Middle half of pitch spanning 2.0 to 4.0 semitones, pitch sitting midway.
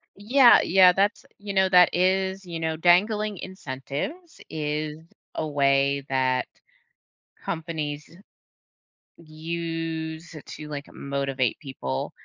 No: average, 4.7 semitones; medium, 160 Hz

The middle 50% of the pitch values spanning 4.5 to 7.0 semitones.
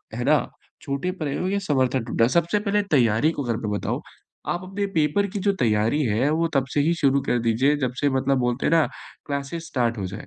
Yes: average, 5.2 semitones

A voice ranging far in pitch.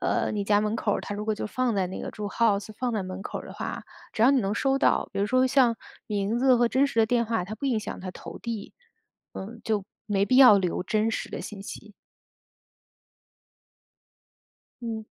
No: average, 3.0 semitones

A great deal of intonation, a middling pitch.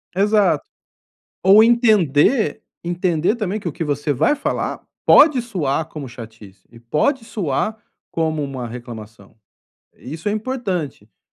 Yes: wide, 8.1 semitones; medium, 165 Hz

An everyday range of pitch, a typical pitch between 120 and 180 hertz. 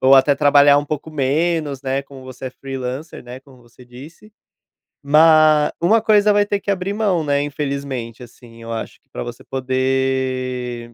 Yes: average, 3.3 semitones; low, 135 Hz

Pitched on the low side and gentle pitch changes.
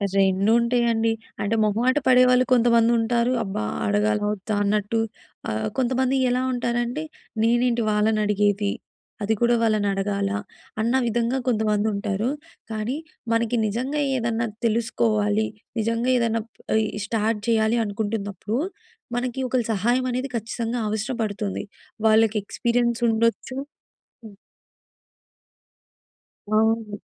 No: high, 225 Hz; narrow, 2.3 semitones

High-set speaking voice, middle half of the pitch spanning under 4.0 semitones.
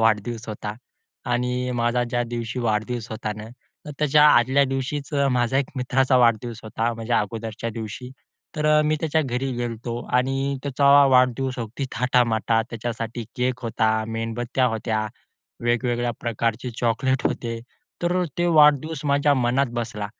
No: low, 120 Hz; average, 2.8 semitones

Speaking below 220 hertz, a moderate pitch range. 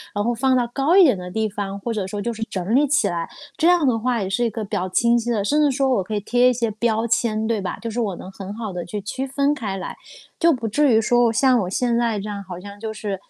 No: high, 225 Hz; average, 3.5 semitones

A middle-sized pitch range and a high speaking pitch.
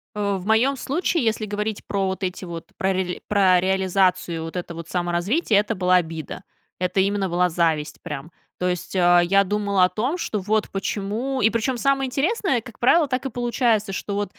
Yes: average, 4.1 semitones; high, 200 Hz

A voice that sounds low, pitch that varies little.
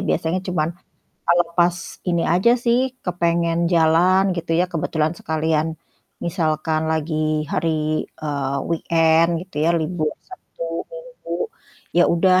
No: medium, 165 Hz; narrow, 1.8 semitones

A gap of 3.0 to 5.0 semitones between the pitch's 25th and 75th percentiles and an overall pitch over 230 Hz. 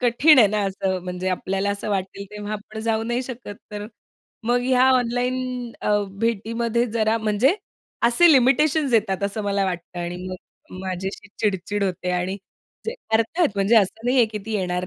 No: average, 3.8 semitones; high, 215 Hz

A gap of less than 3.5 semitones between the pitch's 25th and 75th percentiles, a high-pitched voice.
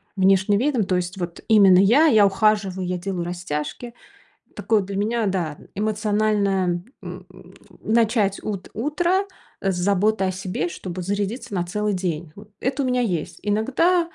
Yes: average, 3.1 semitones; high, 200 Hz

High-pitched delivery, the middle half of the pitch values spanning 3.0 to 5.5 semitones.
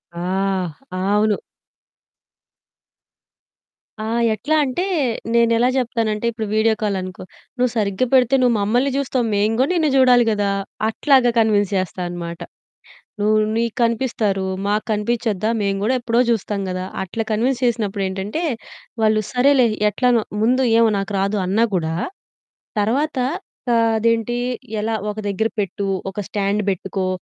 Yes: high, 220 Hz; average, 3.3 semitones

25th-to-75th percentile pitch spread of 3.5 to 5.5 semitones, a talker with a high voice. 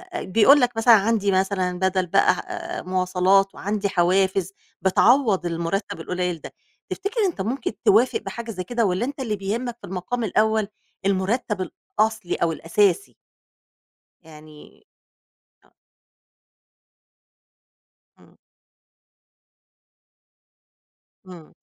Yes: average, 3.8 semitones; high, 195 Hz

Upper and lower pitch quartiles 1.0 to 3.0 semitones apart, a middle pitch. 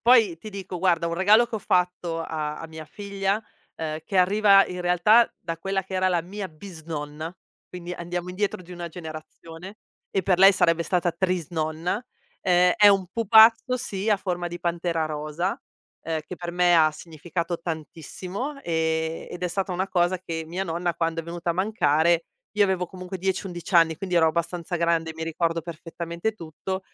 Yes: narrow, 2.6 semitones; medium, 175 Hz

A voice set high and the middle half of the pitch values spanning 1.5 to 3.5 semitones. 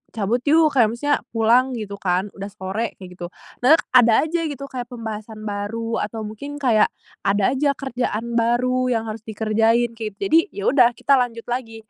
Yes: high, 230 Hz; average, 2.9 semitones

